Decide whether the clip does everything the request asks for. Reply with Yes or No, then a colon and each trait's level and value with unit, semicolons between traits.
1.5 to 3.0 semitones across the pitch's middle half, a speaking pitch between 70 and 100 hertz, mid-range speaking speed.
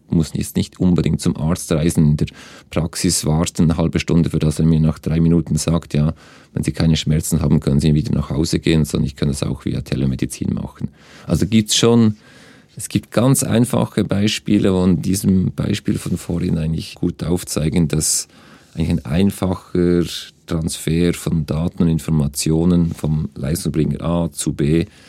Yes: narrow, 2.4 semitones; very low, 80 Hz; average, 180 wpm